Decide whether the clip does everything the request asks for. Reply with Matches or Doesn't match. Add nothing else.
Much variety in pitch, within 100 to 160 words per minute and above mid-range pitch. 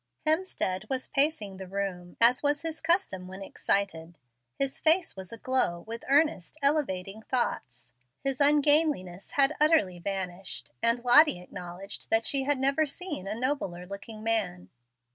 Matches